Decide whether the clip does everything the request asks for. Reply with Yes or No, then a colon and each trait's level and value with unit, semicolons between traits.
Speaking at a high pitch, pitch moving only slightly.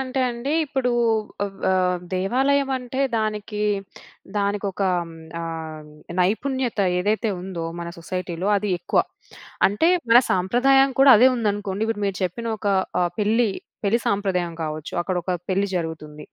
No: high, 205 Hz; average, 4.8 semitones